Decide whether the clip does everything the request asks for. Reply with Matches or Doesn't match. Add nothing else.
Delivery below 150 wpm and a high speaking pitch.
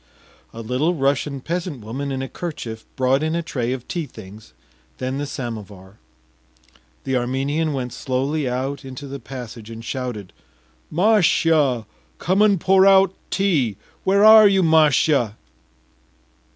Doesn't match